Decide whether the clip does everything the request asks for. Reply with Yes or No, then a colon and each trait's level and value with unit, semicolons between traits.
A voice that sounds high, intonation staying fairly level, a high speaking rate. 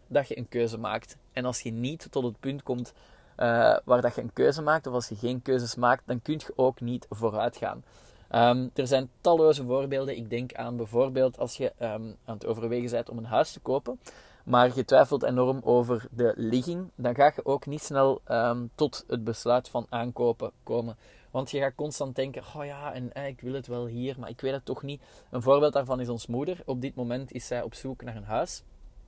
No: low, 125 Hz; narrow, 2.3 semitones; fast, 225 wpm